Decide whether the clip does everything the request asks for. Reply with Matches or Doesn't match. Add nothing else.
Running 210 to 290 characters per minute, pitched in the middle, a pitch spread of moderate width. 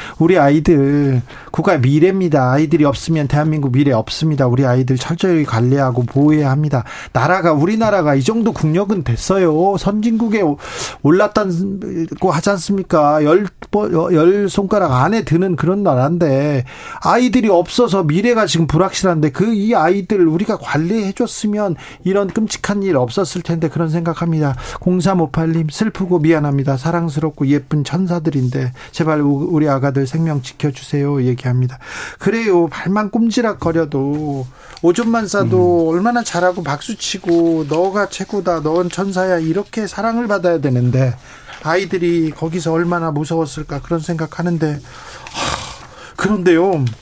Doesn't match